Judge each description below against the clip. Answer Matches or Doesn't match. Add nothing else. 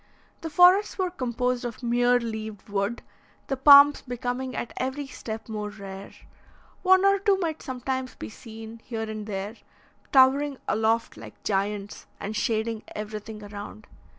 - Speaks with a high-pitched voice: Matches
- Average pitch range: Matches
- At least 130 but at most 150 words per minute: Matches